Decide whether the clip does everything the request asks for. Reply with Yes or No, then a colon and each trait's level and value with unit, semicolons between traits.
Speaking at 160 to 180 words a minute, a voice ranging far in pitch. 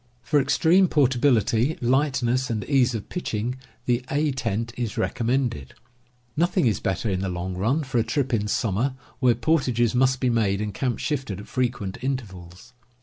No: average, 175 wpm; average, 3.8 semitones